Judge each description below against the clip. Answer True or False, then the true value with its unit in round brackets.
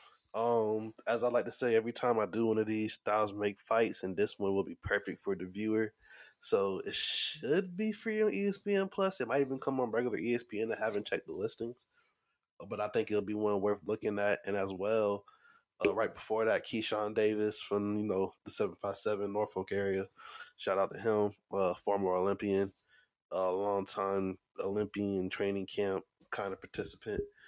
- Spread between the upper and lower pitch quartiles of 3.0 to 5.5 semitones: True (5.0 semitones)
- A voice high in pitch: False (105 Hz)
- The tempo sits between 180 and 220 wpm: True (190 wpm)